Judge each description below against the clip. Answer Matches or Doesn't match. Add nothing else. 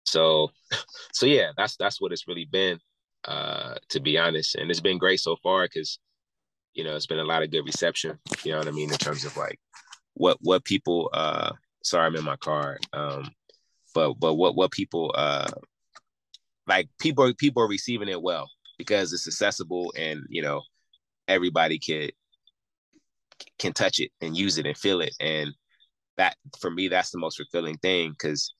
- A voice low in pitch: Matches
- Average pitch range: Matches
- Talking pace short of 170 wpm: Doesn't match